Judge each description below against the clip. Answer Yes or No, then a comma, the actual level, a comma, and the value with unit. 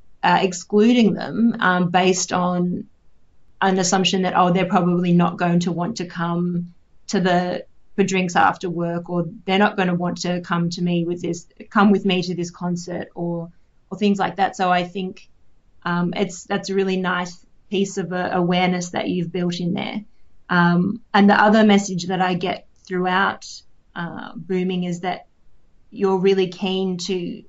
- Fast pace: No, average, 180 wpm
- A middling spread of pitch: No, narrow, 1.7 semitones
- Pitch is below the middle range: No, medium, 180 Hz